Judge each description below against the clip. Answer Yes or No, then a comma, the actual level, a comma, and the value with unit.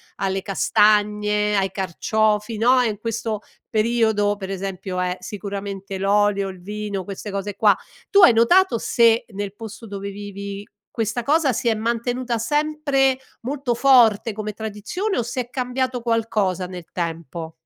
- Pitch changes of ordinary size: Yes, average, 3.1 semitones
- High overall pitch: Yes, high, 210 Hz